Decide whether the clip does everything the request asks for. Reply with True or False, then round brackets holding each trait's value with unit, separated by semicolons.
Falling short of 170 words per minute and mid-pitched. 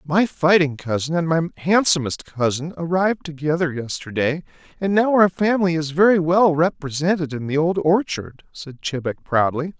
True (155 wpm; 160 Hz)